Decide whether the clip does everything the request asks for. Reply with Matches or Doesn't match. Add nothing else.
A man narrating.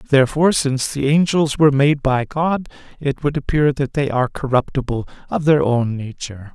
Matches